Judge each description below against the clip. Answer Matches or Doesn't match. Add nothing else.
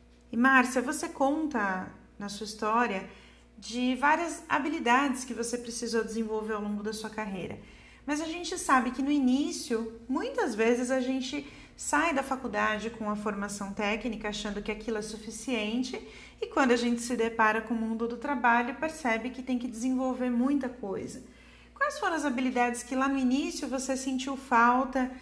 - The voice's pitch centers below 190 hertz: Doesn't match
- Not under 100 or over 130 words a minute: Doesn't match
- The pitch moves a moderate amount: Matches